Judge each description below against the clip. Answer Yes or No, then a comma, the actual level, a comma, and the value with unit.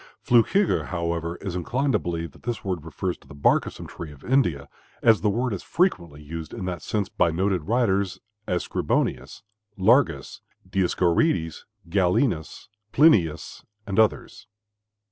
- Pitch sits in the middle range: No, very low, 90 Hz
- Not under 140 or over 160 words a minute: Yes, average, 150 wpm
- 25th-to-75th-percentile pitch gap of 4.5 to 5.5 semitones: Yes, average, 5.2 semitones